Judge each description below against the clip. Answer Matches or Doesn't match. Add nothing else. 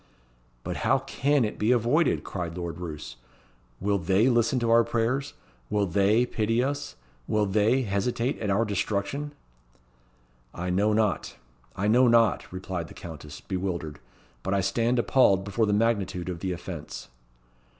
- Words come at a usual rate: Matches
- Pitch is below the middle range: Matches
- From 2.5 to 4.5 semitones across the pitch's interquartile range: Matches